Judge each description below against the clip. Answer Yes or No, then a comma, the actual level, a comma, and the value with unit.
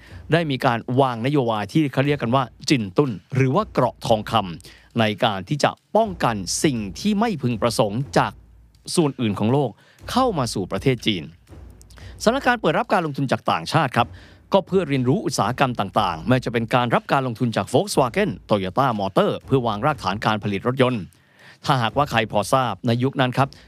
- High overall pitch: No, low, 125 Hz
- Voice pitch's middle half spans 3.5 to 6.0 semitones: Yes, average, 4.9 semitones